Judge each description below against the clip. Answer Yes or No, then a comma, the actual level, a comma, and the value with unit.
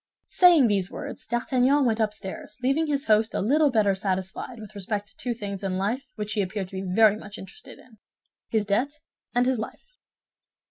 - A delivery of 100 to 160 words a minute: No, average, 175 wpm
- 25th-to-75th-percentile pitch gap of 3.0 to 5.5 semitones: Yes, average, 4.3 semitones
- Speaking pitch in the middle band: No, high, 215 Hz